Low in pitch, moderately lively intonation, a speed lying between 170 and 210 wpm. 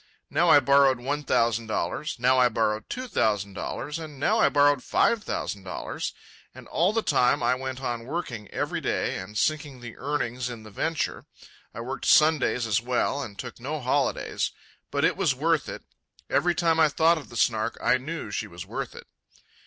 Yes: low, 130 Hz; average, 4.6 semitones; average, 195 wpm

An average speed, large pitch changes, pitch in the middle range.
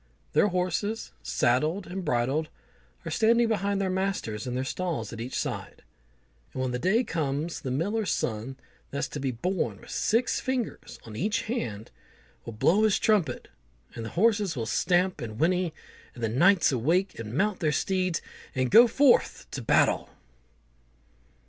Yes: average, 160 wpm; wide, 7.9 semitones; medium, 175 Hz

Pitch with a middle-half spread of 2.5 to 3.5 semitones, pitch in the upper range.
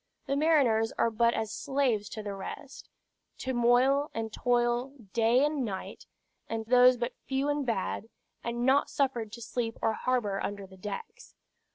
Yes: average, 3.2 semitones; high, 240 Hz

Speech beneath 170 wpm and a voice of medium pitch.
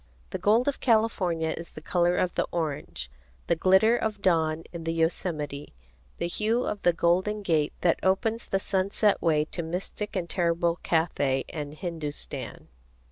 Yes: average, 160 wpm; medium, 175 Hz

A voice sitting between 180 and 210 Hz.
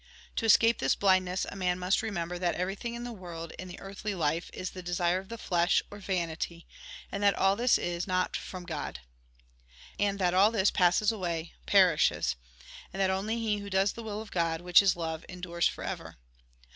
Yes: medium, 185 Hz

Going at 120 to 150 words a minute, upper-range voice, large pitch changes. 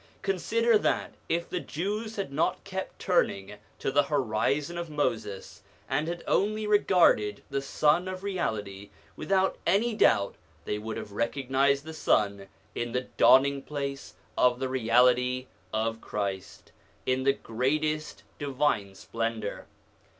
No: slow, 135 wpm; medium, 140 Hz; wide, 7.1 semitones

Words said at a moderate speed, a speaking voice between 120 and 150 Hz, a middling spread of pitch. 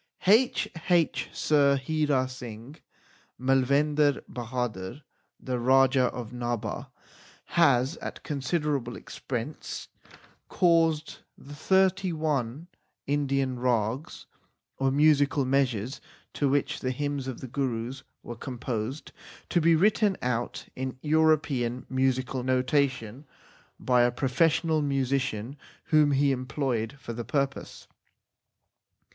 No: slow, 105 wpm; low, 135 Hz; average, 3.2 semitones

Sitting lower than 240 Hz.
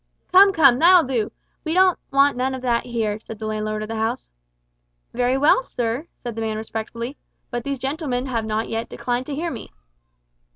No: high, 245 Hz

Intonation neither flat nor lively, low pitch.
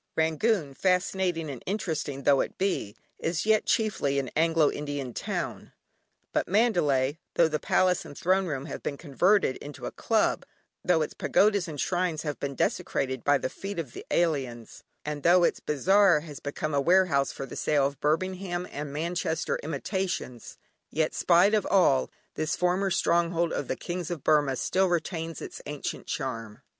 No: average, 4.3 semitones; medium, 160 Hz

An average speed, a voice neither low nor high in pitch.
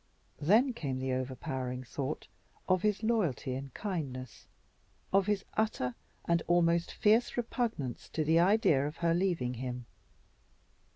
No: slow, 130 wpm; medium, 165 Hz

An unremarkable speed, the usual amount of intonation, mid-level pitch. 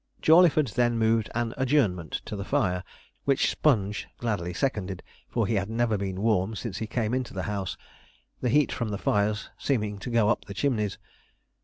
No: average, 180 wpm; average, 3.5 semitones; low, 110 Hz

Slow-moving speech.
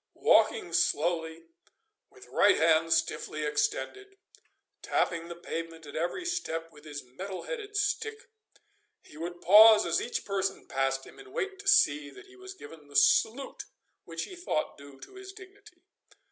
No: average, 160 wpm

